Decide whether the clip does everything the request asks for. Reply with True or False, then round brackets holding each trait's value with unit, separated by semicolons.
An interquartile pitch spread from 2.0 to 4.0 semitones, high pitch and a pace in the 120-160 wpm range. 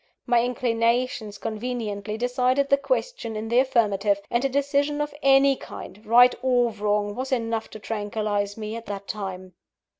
True (3.4 semitones; 230 Hz; 155 wpm)